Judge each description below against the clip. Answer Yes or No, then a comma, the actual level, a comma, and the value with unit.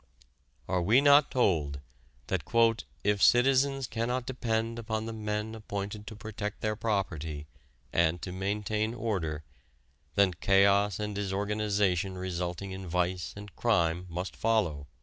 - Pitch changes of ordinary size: Yes, average, 3.4 semitones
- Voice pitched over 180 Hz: No, low, 100 Hz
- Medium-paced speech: No, slow, 130 wpm